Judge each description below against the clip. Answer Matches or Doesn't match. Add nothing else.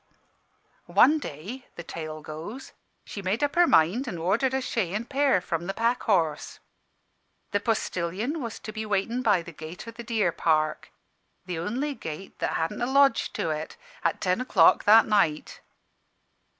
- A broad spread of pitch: Matches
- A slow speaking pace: Doesn't match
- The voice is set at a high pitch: Matches